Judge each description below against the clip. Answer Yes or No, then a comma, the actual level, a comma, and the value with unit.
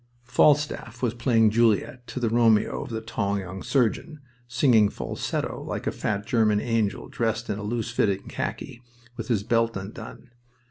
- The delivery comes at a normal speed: Yes, average, 155 wpm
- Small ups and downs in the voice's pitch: Yes, narrow, 2.2 semitones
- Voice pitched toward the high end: No, low, 115 Hz